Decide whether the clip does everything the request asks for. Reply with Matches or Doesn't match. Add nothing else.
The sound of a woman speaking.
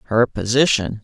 Doesn't match